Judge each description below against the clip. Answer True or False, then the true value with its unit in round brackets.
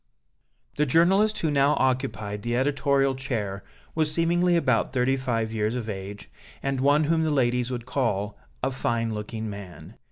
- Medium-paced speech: True (160 wpm)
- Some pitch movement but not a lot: True (4.7 semitones)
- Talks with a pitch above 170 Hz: False (130 Hz)